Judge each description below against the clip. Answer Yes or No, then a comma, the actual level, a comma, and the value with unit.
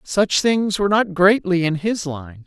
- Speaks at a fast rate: No, average, 195 wpm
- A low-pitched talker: No, high, 190 Hz